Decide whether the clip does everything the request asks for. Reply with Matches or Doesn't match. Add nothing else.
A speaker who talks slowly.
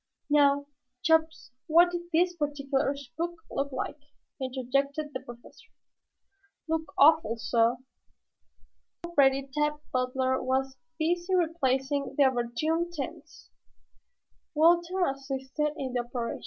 Matches